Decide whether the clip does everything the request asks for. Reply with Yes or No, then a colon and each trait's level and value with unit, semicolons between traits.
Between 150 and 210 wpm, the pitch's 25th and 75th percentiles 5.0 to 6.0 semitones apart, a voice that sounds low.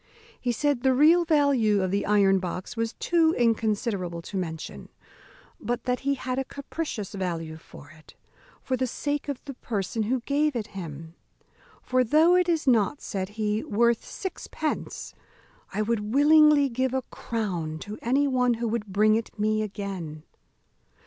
No: average, 160 wpm; wide, 5.6 semitones; high, 230 Hz